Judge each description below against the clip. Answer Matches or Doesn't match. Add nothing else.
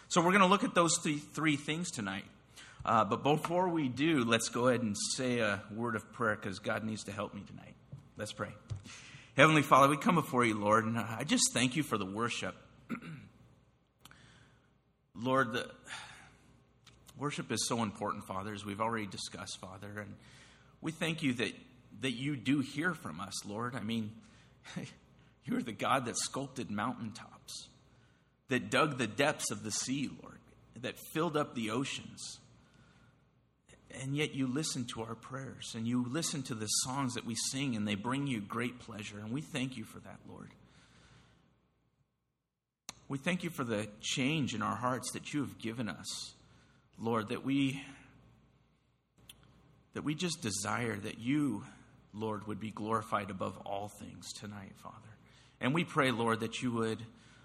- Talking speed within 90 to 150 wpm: Doesn't match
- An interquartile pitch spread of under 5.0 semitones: Matches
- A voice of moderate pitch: Doesn't match